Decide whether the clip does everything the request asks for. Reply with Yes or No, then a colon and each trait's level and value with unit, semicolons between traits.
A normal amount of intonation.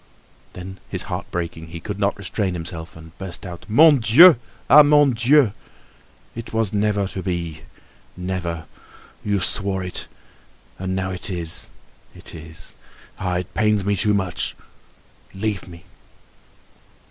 Yes: average, 3.4 semitones